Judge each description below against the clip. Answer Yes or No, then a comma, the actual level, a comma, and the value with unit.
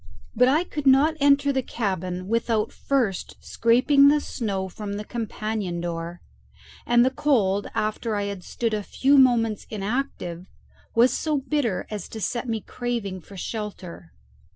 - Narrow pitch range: No, average, 4.9 semitones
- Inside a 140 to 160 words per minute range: Yes, average, 155 wpm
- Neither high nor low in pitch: No, high, 225 Hz